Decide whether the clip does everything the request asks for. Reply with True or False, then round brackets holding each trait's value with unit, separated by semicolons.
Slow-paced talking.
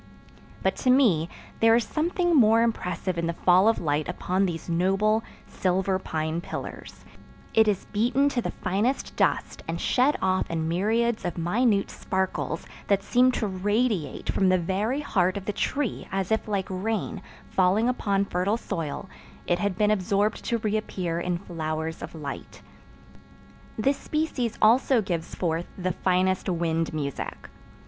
False (155 wpm)